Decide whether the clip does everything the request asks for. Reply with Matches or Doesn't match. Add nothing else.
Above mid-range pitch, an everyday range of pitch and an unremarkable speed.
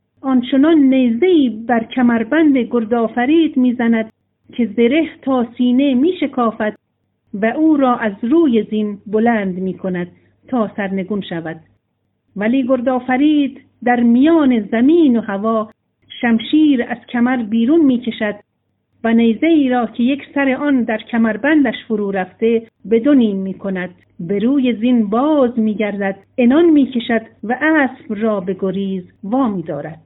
Matches